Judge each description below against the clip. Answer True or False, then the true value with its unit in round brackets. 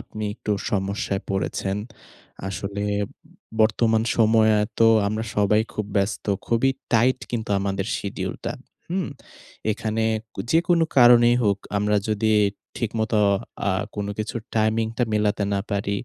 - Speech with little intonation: True (2.0 semitones)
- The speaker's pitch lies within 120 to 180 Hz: False (110 Hz)